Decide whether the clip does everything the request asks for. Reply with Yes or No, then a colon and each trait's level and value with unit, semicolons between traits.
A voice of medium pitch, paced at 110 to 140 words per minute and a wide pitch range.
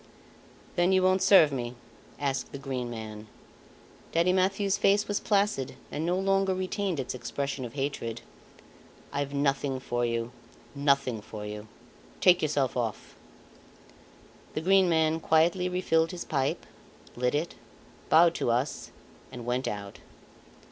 Yes: medium, 145 Hz; slow, 135 wpm; wide, 6.6 semitones